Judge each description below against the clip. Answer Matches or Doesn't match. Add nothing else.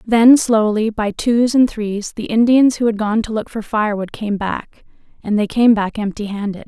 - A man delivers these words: Doesn't match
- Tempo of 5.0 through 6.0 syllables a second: Doesn't match